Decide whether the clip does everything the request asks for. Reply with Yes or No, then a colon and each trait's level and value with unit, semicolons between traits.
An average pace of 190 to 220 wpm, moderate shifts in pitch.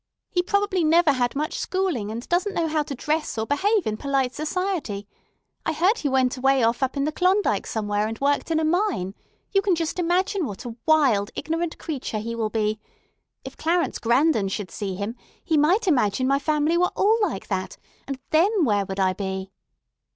No: average, 195 wpm; wide, 7.7 semitones